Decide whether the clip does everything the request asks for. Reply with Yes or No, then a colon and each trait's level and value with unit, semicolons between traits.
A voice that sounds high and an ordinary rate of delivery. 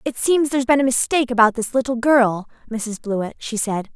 No: high, 240 Hz; fast, 210 wpm